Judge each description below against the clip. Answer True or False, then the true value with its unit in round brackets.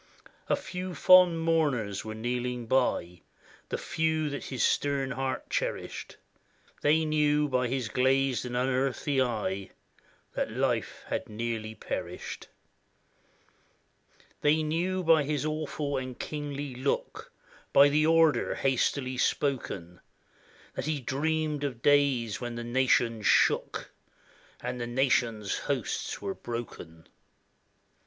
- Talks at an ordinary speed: False (120 wpm)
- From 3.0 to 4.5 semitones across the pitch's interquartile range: True (4.0 semitones)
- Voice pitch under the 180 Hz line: True (135 Hz)